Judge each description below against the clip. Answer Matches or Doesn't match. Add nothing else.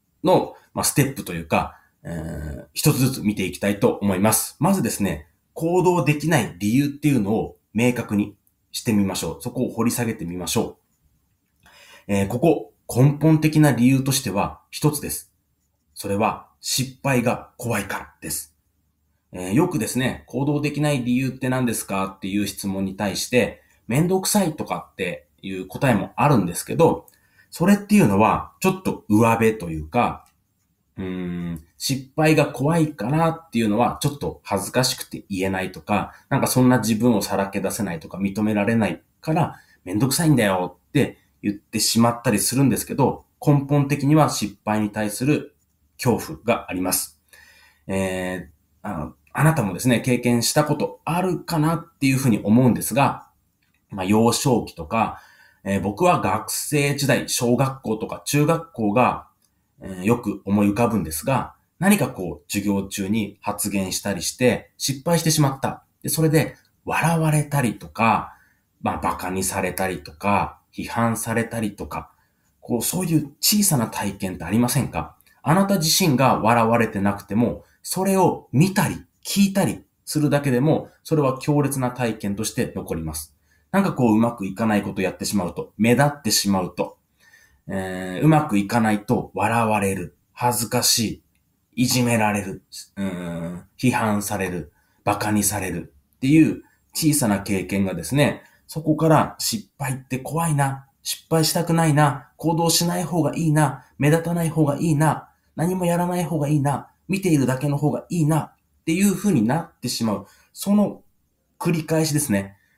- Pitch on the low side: Matches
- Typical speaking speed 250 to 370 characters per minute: Matches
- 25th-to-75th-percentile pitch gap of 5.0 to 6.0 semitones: Doesn't match